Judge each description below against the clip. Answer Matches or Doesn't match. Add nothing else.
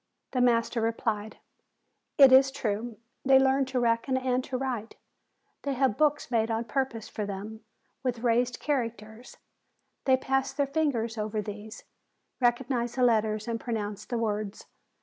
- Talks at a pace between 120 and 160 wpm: Matches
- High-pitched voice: Matches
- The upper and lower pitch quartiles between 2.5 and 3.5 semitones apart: Matches